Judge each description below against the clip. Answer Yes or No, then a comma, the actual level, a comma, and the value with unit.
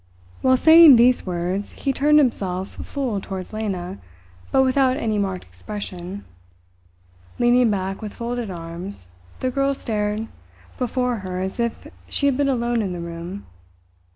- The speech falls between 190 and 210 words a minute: No, average, 145 wpm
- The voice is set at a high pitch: Yes, high, 215 Hz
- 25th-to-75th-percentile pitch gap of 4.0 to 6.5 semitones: Yes, average, 5.2 semitones